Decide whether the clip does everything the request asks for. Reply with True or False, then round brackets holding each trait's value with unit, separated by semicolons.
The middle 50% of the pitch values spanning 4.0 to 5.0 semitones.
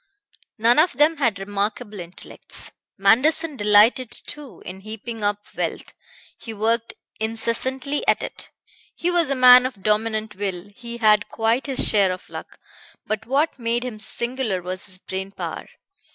False (3.6 semitones)